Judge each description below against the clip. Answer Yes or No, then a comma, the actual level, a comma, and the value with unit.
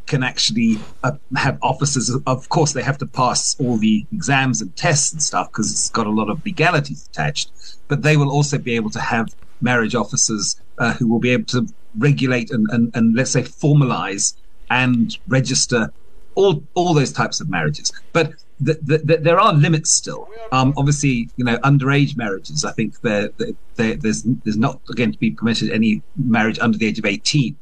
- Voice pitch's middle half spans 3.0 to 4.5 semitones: Yes, average, 4.1 semitones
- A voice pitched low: Yes, low, 130 Hz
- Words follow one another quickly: No, average, 190 wpm